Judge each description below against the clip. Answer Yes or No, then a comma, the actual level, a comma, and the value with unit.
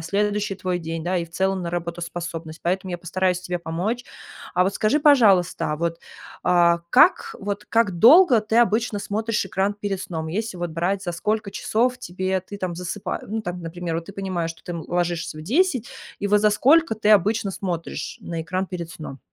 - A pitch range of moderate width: Yes, average, 3.5 semitones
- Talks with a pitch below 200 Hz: Yes, medium, 185 Hz